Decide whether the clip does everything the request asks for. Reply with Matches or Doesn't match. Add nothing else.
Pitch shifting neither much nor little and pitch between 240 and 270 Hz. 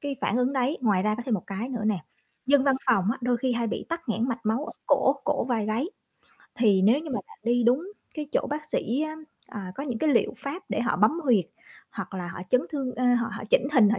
Matches